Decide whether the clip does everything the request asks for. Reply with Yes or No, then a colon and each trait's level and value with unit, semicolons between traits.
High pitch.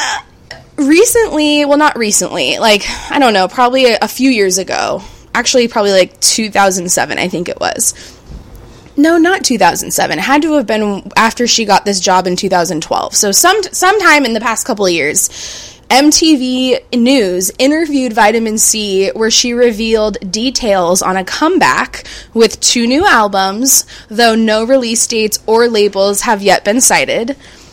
Yes: high, 230 Hz